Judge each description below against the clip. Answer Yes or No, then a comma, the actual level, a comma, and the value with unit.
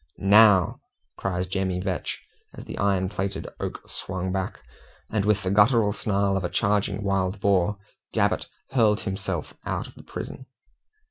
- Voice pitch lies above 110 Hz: No, low, 100 Hz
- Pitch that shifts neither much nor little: No, narrow, 1.6 semitones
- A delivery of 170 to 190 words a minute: No, average, 150 wpm